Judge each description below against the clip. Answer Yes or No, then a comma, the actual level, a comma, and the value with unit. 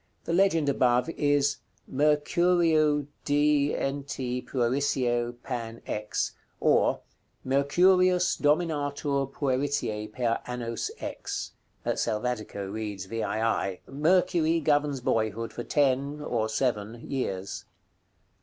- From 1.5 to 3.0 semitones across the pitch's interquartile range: No, average, 4.3 semitones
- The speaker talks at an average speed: No, slow, 90 wpm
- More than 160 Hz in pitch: No, low, 135 Hz